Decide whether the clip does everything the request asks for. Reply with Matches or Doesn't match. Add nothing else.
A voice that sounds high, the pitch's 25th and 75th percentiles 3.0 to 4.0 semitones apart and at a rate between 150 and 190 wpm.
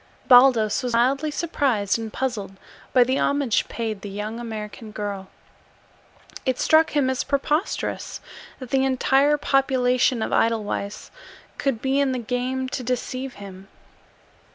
Doesn't match